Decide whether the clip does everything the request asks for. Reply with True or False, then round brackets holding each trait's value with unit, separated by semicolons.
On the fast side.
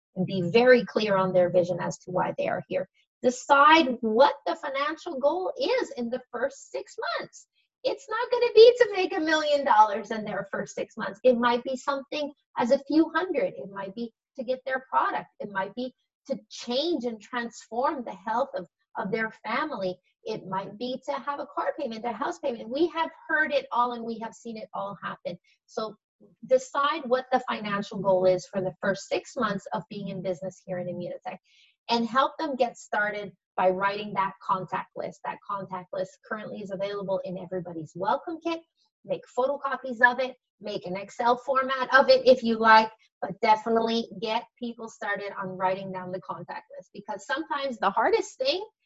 False (195 wpm)